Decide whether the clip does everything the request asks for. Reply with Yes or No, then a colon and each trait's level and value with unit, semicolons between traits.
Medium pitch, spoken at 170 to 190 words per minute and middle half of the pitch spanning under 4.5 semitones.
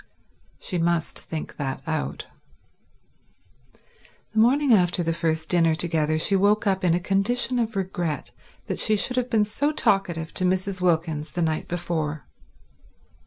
No: medium, 175 Hz; average, 150 wpm; average, 4.0 semitones